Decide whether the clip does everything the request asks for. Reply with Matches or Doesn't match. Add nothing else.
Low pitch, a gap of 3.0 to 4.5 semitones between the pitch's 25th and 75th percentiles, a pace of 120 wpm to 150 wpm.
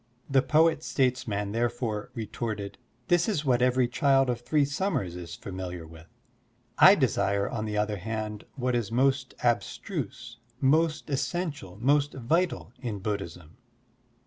Doesn't match